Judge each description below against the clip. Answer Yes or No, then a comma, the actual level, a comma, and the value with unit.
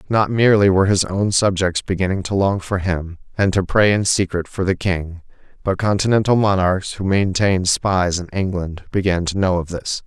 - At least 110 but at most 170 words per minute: No, average, 190 wpm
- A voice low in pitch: Yes, very low, 95 Hz